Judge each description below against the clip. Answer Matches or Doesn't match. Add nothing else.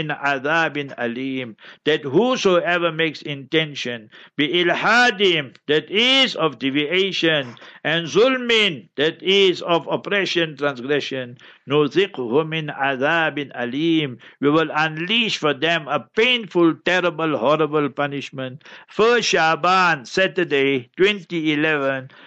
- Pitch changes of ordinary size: Matches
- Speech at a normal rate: Doesn't match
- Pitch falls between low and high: Matches